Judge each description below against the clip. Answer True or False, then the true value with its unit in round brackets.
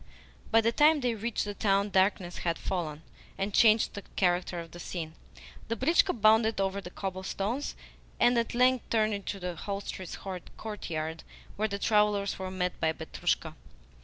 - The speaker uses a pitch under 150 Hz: False (200 Hz)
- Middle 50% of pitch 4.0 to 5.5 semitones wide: False (3.5 semitones)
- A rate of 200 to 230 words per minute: False (160 wpm)